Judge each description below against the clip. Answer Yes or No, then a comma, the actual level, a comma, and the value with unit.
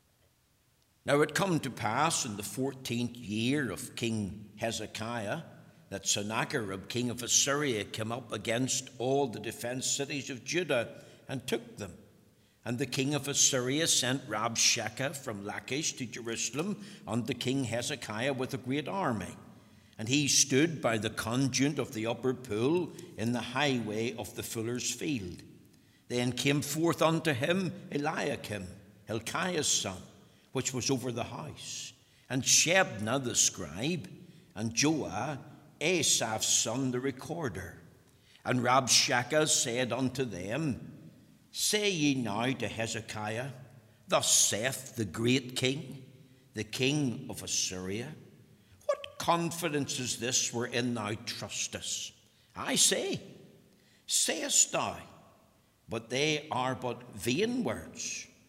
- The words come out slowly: Yes, slow, 125 wpm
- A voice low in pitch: Yes, low, 125 Hz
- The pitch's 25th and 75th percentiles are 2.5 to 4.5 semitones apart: Yes, average, 3.7 semitones